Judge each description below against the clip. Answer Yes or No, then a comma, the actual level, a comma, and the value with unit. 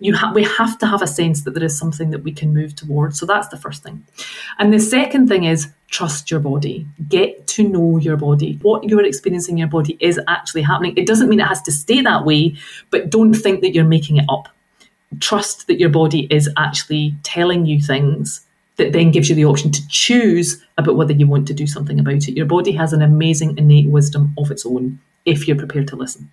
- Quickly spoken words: Yes, fast, 235 wpm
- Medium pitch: Yes, medium, 160 Hz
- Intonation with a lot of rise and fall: No, average, 4.6 semitones